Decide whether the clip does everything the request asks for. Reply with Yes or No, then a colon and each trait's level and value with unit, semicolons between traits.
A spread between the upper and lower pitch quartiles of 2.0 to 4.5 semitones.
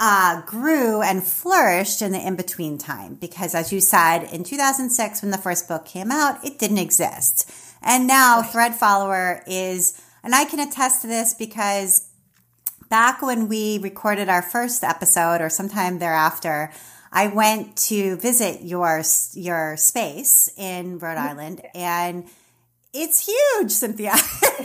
No: average, 5.0 semitones